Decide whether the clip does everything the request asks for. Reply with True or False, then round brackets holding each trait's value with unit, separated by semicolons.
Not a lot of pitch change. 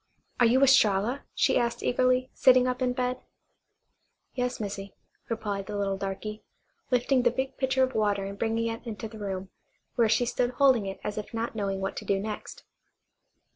False (3.7 semitones)